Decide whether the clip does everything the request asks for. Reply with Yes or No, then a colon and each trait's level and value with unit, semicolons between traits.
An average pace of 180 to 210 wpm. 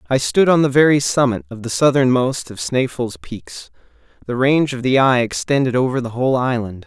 Yes: average, 190 wpm